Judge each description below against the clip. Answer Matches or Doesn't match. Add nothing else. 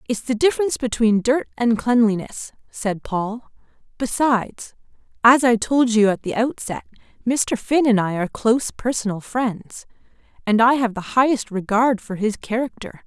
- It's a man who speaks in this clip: Doesn't match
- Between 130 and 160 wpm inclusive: Matches